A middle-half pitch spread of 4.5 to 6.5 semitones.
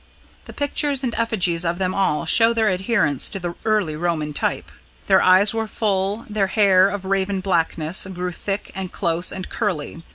No: average, 3.3 semitones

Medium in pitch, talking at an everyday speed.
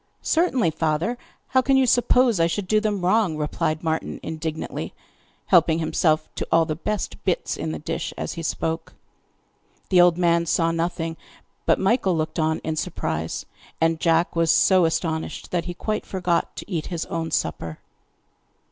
Yes: medium, 165 Hz; average, 165 wpm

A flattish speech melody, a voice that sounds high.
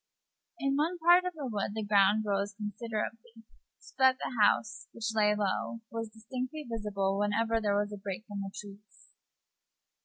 Yes: narrow, 2.2 semitones; high, 215 Hz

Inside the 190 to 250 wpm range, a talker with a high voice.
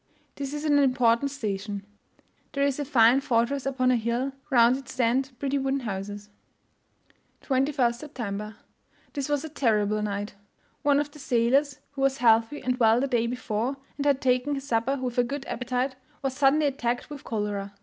No: average, 175 wpm; very high, 255 Hz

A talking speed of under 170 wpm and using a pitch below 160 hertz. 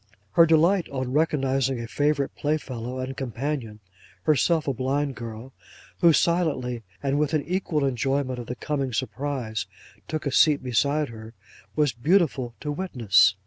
Yes: average, 140 wpm; low, 135 Hz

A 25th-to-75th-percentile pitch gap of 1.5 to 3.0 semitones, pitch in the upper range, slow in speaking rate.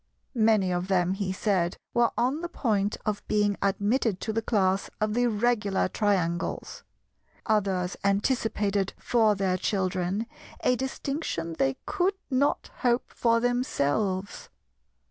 No: average, 4.0 semitones; high, 205 Hz; slow, 125 wpm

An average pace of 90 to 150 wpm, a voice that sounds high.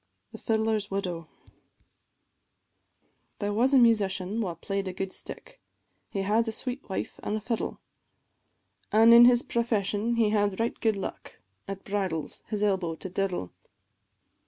Yes: average, 145 wpm; high, 205 Hz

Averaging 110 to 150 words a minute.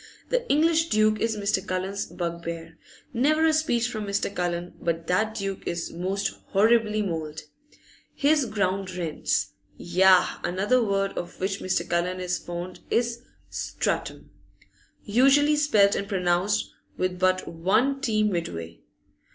Yes: slow, 135 wpm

